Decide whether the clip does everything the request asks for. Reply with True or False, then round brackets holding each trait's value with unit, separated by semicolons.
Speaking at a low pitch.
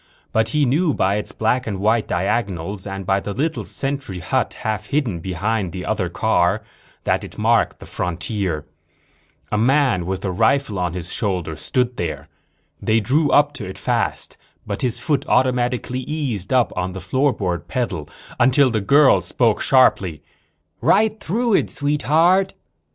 True (110 Hz)